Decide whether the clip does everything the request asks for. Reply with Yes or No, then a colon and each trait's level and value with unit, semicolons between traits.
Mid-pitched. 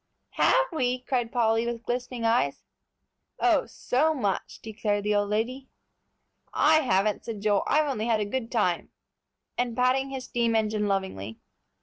No: high, 230 Hz